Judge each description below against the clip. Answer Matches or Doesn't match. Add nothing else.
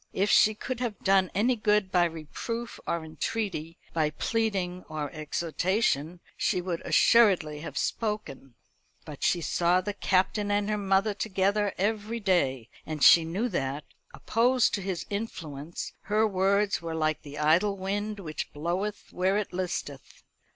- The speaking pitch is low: Doesn't match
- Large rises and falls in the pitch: Doesn't match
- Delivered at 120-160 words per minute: Matches